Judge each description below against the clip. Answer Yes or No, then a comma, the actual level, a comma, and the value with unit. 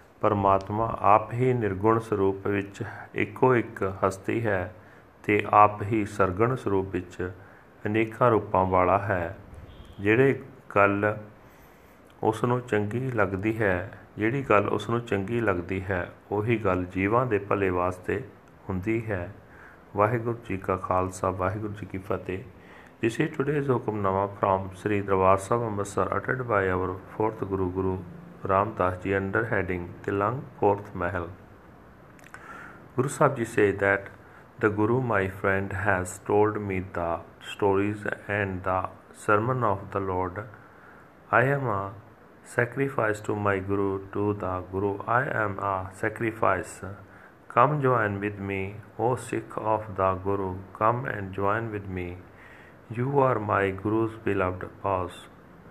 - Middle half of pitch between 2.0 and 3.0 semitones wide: Yes, narrow, 2.5 semitones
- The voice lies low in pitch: Yes, low, 100 Hz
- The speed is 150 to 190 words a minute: No, average, 135 wpm